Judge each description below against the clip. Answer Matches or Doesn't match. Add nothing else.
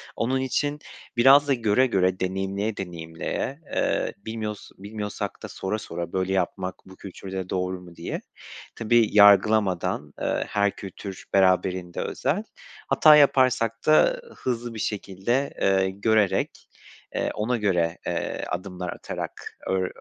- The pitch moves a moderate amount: Matches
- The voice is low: Matches